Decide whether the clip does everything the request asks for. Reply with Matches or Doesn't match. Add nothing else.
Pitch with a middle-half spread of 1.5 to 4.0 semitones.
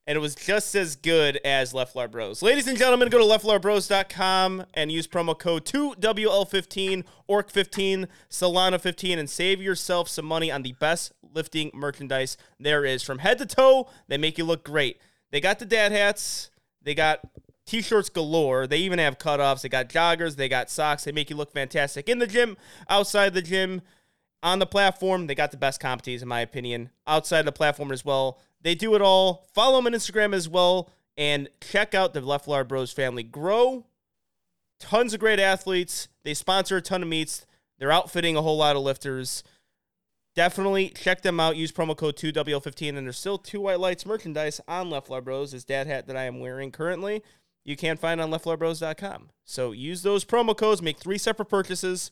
Doesn't match